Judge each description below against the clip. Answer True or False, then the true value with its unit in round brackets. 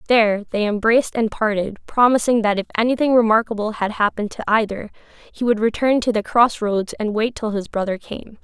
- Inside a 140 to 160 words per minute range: False (190 wpm)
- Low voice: False (220 Hz)